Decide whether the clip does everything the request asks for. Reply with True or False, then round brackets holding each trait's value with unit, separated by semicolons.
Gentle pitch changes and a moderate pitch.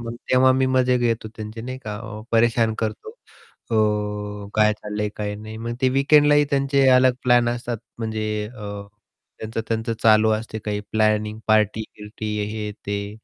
False (2.3 semitones; 110 Hz)